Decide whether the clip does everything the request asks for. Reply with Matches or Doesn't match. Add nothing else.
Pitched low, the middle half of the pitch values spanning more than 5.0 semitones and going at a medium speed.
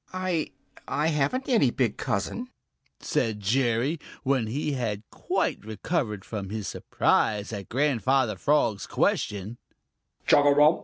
Doesn't match